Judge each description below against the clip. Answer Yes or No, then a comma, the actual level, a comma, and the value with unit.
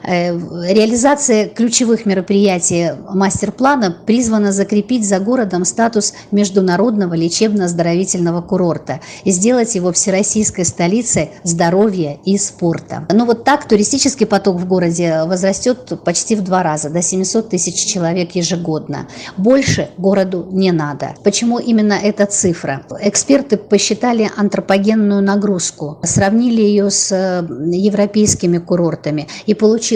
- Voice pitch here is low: No, high, 195 Hz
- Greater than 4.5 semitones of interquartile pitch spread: No, average, 3.5 semitones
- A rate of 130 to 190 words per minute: No, slow, 110 wpm